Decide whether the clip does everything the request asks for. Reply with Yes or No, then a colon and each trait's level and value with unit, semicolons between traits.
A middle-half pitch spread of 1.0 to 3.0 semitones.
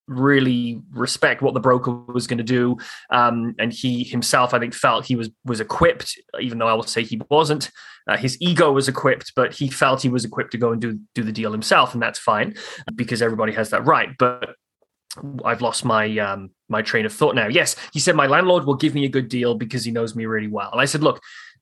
Yes: narrow, 2.5 semitones